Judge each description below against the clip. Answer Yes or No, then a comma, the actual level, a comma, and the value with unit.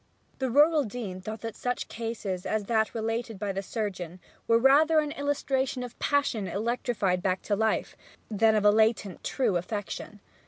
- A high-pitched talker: Yes, high, 220 Hz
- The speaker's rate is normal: Yes, average, 165 wpm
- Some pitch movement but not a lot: Yes, average, 3.6 semitones